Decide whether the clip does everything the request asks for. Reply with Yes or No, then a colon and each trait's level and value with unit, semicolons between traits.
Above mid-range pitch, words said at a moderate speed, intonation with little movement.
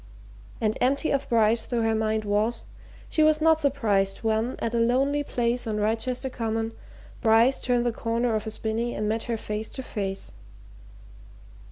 Yes: high, 230 Hz; average, 170 wpm; narrow, 2.3 semitones